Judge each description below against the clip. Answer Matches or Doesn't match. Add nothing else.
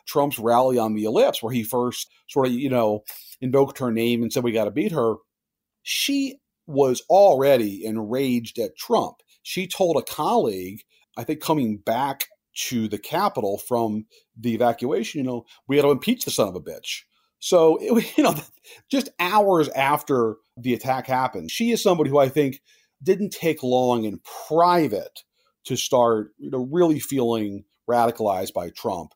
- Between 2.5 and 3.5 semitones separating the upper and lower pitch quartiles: Doesn't match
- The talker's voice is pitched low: Matches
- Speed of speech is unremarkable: Matches